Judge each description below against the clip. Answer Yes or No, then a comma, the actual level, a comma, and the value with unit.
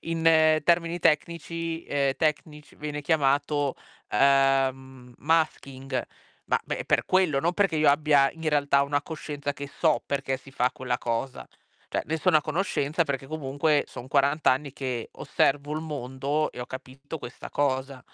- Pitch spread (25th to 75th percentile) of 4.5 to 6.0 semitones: No, average, 2.7 semitones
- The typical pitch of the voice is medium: Yes, medium, 145 Hz